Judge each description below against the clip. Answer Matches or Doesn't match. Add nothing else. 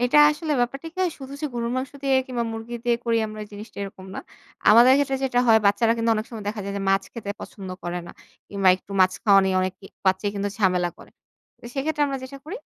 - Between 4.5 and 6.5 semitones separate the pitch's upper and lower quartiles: Matches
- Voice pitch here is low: Doesn't match